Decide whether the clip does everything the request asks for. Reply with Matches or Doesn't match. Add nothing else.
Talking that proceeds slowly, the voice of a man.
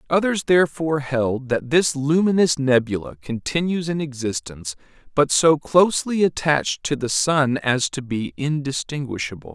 Matches